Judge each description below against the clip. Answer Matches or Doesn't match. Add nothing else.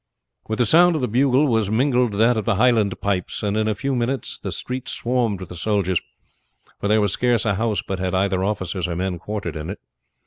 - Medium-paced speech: Doesn't match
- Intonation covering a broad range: Doesn't match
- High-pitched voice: Doesn't match